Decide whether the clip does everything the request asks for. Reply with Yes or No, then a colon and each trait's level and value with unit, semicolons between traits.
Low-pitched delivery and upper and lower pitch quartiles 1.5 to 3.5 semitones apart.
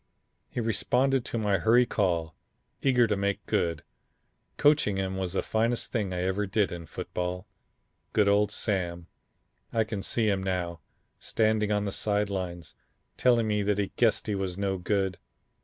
Yes: low, 100 Hz; average, 2.9 semitones